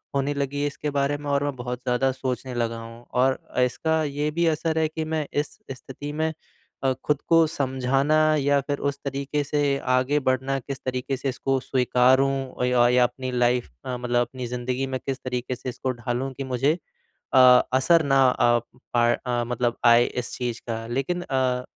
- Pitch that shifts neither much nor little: No, narrow, 2.3 semitones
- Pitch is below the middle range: Yes, low, 130 Hz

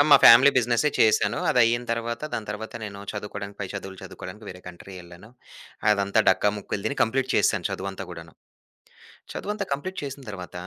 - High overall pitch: No, low, 105 Hz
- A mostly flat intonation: No, average, 3.7 semitones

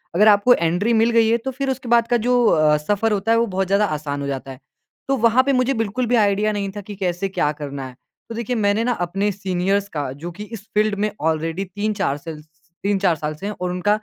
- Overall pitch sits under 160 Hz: No, high, 200 Hz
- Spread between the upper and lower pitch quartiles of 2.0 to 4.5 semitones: No, average, 4.9 semitones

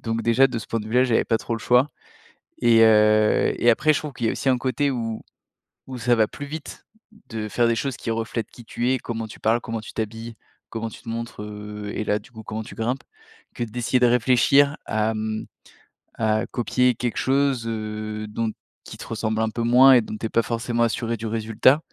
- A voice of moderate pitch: No, low, 115 Hz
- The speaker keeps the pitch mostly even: Yes, narrow, 2.0 semitones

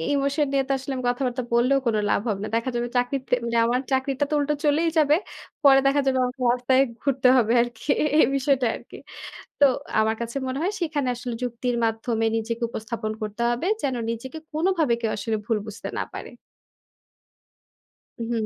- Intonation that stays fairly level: No, average, 3.0 semitones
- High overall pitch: Yes, very high, 250 Hz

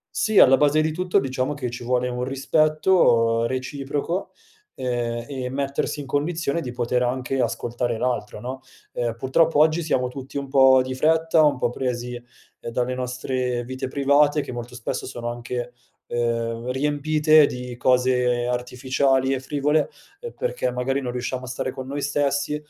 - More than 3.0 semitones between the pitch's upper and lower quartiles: No, narrow, 2.6 semitones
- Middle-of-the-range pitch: No, low, 130 Hz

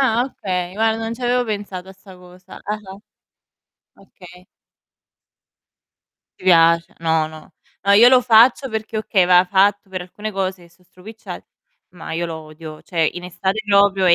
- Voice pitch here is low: No, high, 190 Hz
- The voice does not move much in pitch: No, average, 3.3 semitones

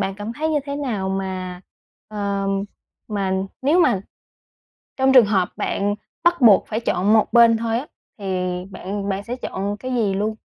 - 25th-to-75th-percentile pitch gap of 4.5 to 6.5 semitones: No, average, 3.9 semitones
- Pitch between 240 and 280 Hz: No, high, 210 Hz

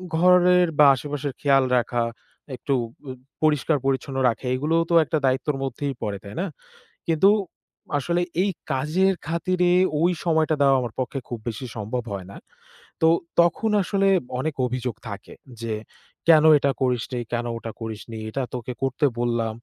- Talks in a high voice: No, low, 135 Hz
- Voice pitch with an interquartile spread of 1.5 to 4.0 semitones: No, average, 5.1 semitones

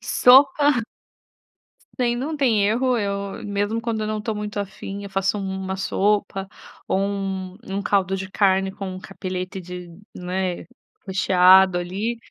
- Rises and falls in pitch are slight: Yes, narrow, 2.2 semitones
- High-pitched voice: Yes, high, 200 Hz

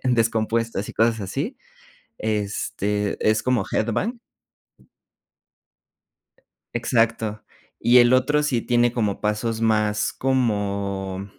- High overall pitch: No, low, 110 Hz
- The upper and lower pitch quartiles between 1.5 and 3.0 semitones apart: Yes, narrow, 2.6 semitones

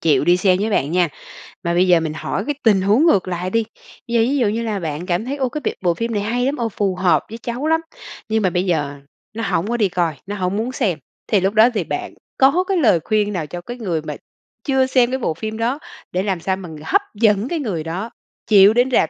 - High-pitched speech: Yes, high, 205 Hz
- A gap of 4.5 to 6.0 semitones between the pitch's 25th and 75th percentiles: Yes, average, 5.1 semitones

